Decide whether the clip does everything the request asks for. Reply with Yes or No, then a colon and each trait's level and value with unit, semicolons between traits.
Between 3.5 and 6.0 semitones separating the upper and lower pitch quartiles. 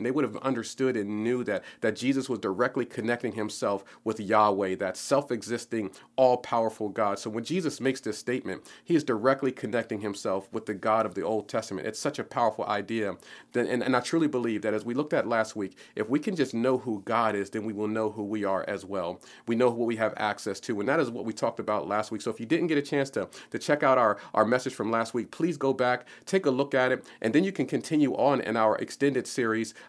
No: average, 3.1 semitones